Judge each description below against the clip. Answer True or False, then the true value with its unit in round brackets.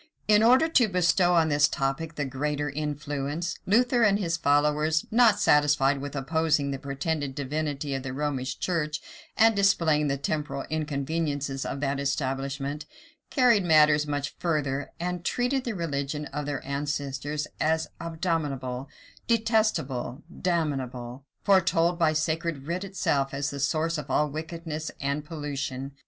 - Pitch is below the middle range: False (150 Hz)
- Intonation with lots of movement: False (3.2 semitones)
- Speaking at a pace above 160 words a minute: False (140 wpm)